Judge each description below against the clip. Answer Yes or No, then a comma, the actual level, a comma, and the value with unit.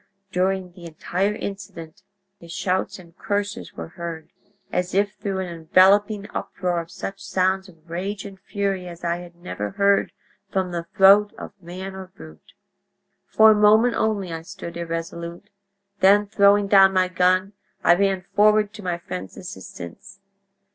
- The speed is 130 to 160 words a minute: Yes, average, 155 wpm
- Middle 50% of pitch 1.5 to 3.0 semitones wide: Yes, average, 2.7 semitones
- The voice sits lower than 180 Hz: No, high, 190 Hz